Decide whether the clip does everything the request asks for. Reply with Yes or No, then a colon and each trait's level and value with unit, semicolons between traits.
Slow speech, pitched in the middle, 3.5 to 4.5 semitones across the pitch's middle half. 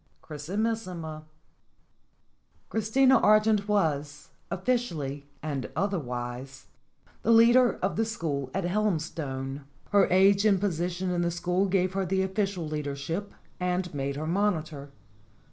No: slow, 125 wpm; medium, 180 Hz; average, 5.3 semitones